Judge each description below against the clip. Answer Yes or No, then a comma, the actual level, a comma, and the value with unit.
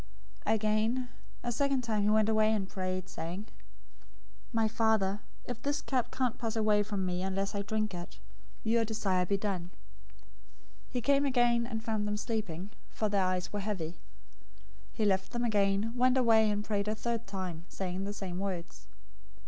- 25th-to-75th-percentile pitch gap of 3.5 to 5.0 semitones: No, average, 2.9 semitones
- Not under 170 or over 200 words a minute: Yes, average, 180 wpm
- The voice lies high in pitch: Yes, high, 215 Hz